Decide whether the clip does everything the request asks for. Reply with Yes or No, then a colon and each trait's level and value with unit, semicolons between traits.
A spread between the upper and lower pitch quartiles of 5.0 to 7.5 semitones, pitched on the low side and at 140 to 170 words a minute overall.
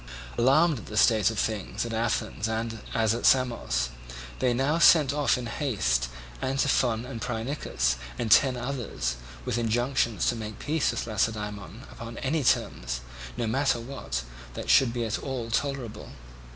No: average, 3.7 semitones; low, 115 Hz; average, 150 wpm